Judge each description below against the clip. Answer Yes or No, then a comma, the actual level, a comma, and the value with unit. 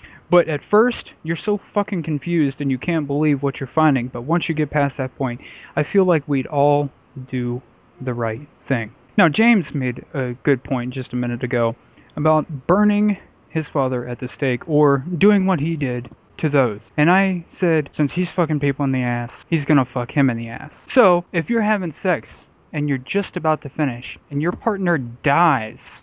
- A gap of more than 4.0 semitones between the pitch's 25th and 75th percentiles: Yes, average, 5.2 semitones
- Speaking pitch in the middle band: Yes, medium, 145 Hz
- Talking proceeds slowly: No, average, 200 wpm